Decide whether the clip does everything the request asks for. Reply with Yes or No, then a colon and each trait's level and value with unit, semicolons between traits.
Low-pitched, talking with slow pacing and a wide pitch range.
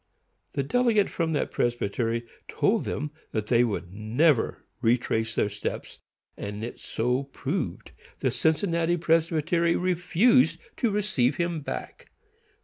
No: medium, 150 Hz; slow, 125 wpm; wide, 6.6 semitones